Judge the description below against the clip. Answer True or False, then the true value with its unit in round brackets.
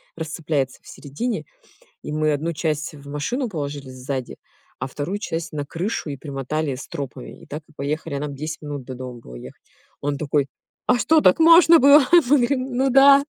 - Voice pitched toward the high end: False (150 Hz)